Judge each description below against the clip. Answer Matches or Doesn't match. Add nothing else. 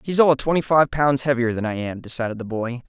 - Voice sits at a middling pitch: Doesn't match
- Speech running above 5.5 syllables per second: Matches